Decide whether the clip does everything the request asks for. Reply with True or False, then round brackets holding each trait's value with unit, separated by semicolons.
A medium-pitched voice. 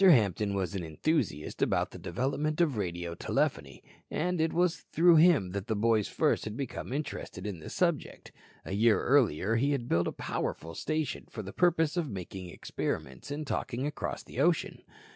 False (120 Hz)